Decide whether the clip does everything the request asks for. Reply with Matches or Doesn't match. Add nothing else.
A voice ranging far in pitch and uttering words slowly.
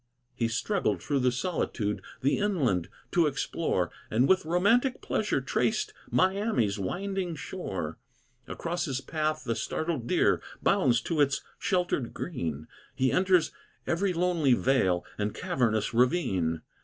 Matches